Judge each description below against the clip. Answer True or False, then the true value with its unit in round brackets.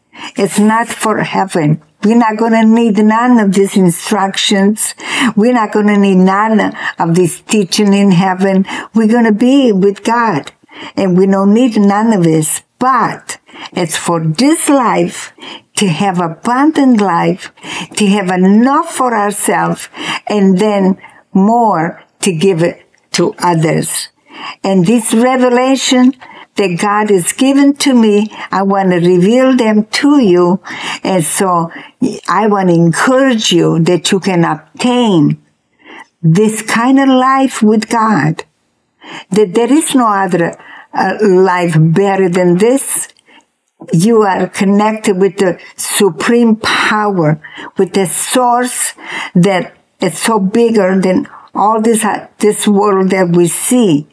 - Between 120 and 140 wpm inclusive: True (135 wpm)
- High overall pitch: True (205 Hz)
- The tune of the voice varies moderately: True (3.9 semitones)